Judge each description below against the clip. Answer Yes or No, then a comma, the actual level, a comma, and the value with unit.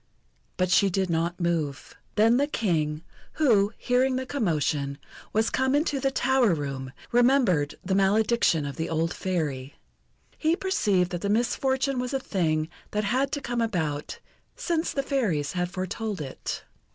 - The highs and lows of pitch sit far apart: Yes, wide, 8.0 semitones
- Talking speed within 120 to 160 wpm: Yes, average, 155 wpm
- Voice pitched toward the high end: Yes, high, 200 Hz